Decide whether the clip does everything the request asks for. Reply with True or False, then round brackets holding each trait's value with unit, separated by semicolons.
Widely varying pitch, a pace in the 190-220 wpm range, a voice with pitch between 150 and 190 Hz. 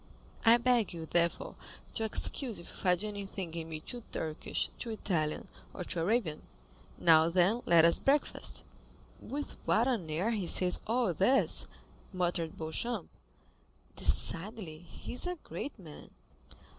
False (5.7 semitones; 145 wpm; 185 Hz)